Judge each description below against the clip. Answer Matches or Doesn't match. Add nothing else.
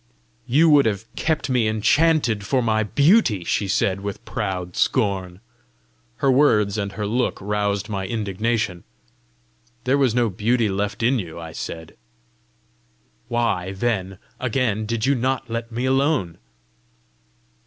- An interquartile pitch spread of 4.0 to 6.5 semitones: Matches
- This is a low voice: Matches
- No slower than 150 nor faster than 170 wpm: Doesn't match